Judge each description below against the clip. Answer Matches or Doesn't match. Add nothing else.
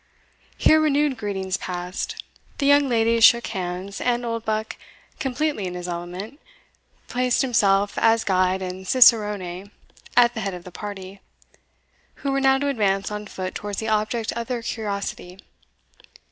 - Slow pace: Doesn't match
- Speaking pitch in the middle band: Doesn't match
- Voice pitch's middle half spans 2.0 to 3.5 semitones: Doesn't match